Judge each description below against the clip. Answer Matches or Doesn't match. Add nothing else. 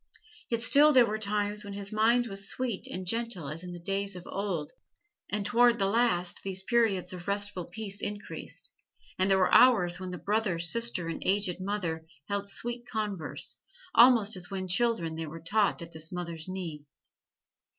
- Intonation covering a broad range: Doesn't match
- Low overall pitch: Doesn't match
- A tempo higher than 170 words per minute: Matches